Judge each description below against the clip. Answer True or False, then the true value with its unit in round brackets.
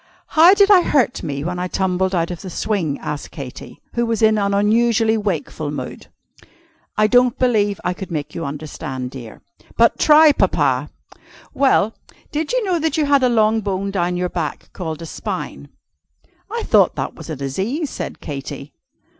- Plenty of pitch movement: True (7.1 semitones)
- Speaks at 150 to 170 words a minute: False (180 wpm)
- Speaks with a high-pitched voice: True (200 Hz)